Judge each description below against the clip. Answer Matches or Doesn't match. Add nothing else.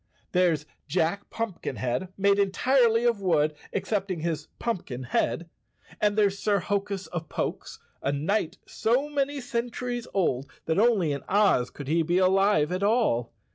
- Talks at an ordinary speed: Matches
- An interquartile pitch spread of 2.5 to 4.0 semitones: Doesn't match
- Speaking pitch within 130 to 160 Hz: Doesn't match